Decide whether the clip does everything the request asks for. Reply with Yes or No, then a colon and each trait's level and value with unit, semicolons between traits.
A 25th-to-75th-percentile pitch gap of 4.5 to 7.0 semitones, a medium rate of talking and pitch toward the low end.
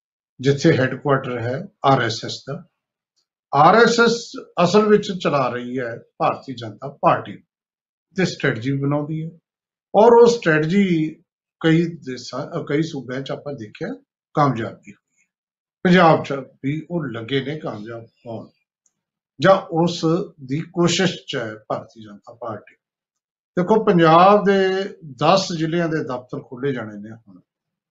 No: wide, 5.4 semitones; average, 125 wpm; medium, 160 Hz